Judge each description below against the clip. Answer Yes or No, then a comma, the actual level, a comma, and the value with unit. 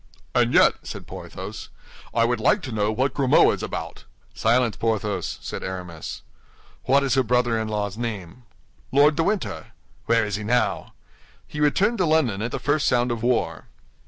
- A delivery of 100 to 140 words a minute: No, average, 175 wpm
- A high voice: No, low, 120 Hz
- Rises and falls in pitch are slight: No, average, 4.3 semitones